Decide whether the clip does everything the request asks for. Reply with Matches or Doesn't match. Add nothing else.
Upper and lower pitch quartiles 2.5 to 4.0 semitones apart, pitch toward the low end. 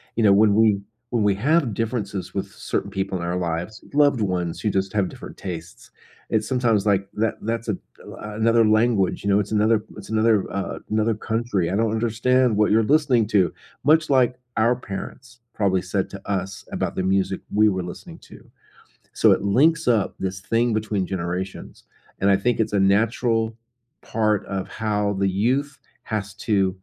Matches